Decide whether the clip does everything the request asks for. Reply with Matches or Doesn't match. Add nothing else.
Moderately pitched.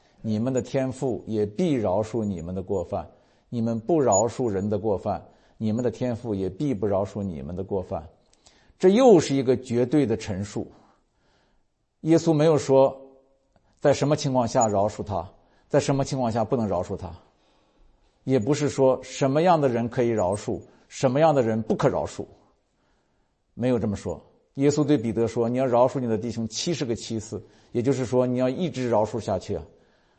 Doesn't match